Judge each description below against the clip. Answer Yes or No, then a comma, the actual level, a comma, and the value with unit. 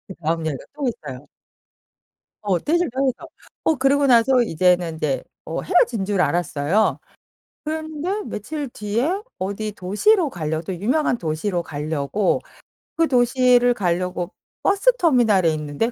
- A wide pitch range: Yes, wide, 8.0 semitones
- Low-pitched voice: No, high, 210 Hz